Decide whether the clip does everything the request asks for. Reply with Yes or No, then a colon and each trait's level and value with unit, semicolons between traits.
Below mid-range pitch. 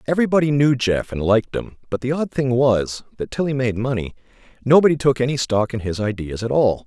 Yes: low, 125 Hz